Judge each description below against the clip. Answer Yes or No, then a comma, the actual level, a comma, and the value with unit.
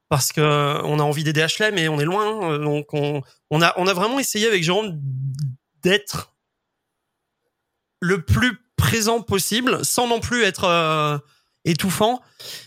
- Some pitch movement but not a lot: No, wide, 6.2 semitones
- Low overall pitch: No, medium, 170 Hz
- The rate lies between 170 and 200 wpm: No, slow, 145 wpm